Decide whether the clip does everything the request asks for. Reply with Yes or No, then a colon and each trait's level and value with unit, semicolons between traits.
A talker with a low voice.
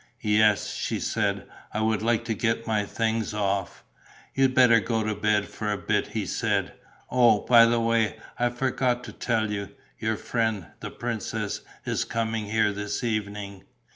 Yes: low, 110 Hz